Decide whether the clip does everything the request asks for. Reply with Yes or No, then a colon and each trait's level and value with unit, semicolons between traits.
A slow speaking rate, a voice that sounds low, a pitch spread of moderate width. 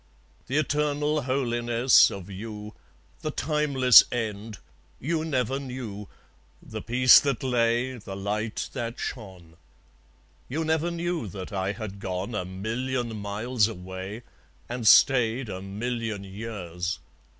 Yes: slow, 120 wpm; low, 115 Hz; average, 4.4 semitones